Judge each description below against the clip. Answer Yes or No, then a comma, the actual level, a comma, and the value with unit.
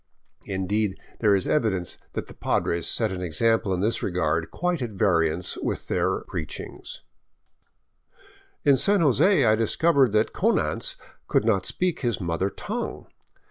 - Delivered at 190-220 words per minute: No, average, 140 wpm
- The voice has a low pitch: Yes, low, 105 Hz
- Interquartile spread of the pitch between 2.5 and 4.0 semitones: No, average, 5.1 semitones